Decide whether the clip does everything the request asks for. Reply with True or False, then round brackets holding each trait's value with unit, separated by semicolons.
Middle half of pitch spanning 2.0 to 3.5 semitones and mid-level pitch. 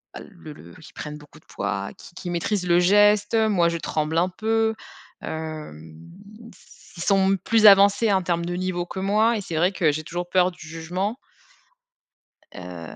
False (4.1 semitones; 175 Hz)